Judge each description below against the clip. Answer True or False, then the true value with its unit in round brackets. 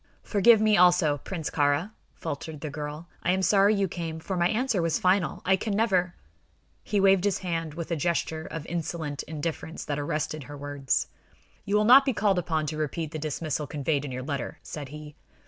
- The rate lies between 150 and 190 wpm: False (200 wpm)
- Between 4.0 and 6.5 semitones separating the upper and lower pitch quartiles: True (4.3 semitones)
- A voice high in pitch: False (165 Hz)